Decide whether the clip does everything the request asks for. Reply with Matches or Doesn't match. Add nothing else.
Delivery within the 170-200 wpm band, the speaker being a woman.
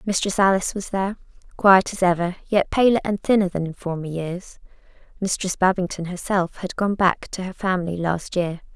Matches